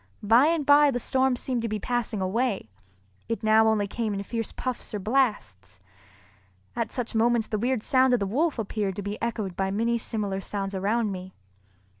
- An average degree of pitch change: Yes, average, 3.4 semitones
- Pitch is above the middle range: Yes, high, 220 Hz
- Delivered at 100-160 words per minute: No, average, 190 wpm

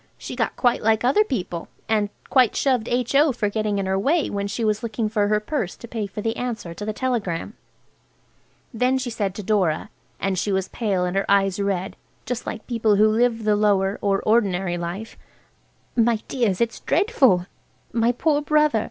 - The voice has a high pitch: Yes, high, 215 Hz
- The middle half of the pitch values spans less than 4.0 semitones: Yes, average, 3.5 semitones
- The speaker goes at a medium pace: Yes, average, 185 wpm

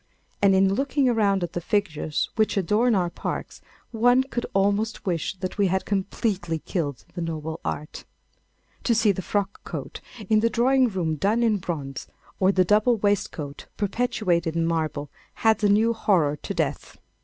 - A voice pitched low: No, high, 195 Hz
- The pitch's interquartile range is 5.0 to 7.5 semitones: No, average, 4.6 semitones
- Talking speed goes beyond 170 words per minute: No, average, 165 wpm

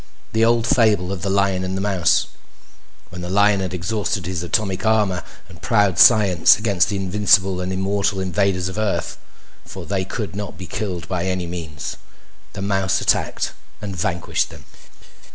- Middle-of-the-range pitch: No, very low, 95 Hz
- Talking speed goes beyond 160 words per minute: Yes, average, 170 wpm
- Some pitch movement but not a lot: No, narrow, 2.0 semitones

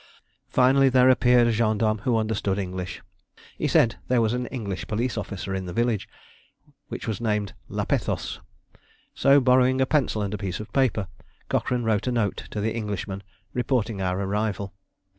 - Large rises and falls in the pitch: No, average, 3.7 semitones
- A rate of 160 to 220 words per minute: Yes, average, 165 wpm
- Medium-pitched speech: No, low, 110 Hz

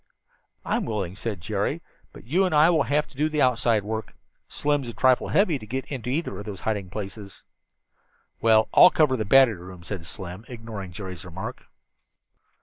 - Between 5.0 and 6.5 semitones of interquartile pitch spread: Yes, wide, 5.5 semitones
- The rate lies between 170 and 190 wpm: Yes, average, 185 wpm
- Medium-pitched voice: No, low, 110 Hz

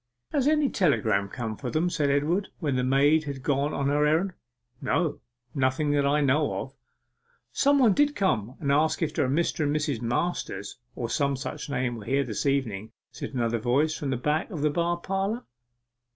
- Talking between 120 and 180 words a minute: No, average, 190 wpm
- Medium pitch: Yes, medium, 145 Hz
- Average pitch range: Yes, average, 4.0 semitones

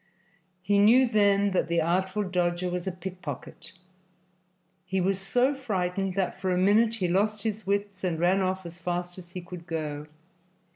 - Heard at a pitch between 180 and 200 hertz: Yes, medium, 185 Hz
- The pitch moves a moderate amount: No, narrow, 2.3 semitones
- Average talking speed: Yes, average, 175 wpm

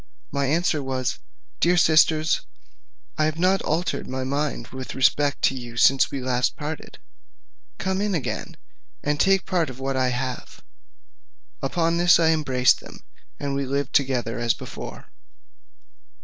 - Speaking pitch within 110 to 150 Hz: Yes, medium, 140 Hz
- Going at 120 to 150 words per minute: Yes, average, 145 wpm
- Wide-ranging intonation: No, average, 3.8 semitones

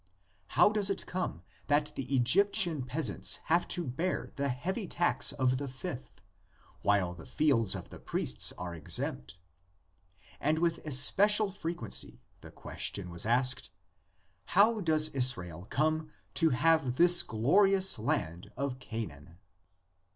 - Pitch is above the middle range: No, medium, 140 Hz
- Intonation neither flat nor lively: No, wide, 7.2 semitones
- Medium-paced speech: No, slow, 130 wpm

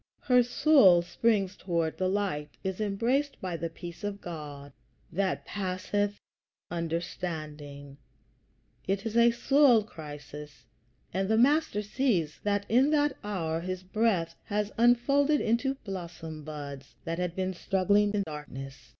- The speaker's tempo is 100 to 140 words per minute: Yes, slow, 135 wpm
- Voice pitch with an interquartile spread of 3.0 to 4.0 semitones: No, average, 5.2 semitones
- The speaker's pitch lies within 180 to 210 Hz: Yes, high, 190 Hz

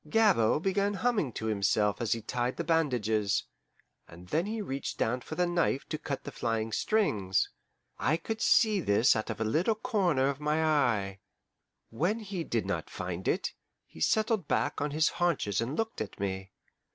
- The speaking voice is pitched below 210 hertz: Yes, medium, 140 Hz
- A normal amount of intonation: No, wide, 8.9 semitones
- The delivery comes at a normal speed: Yes, average, 180 wpm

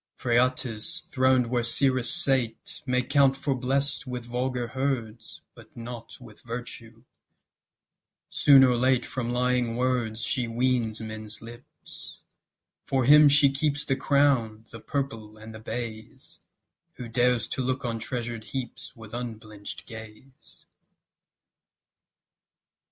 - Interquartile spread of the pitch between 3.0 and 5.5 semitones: No, narrow, 2.4 semitones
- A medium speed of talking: No, slow, 125 wpm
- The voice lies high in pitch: No, low, 120 Hz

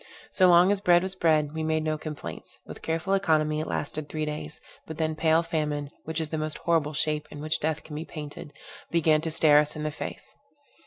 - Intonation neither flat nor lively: No, narrow, 1.3 semitones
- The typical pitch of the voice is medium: Yes, medium, 155 Hz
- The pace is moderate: No, fast, 220 wpm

